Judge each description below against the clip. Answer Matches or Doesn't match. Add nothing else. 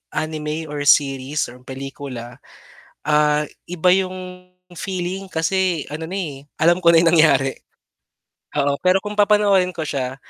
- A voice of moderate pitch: Matches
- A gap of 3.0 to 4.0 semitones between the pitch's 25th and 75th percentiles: Doesn't match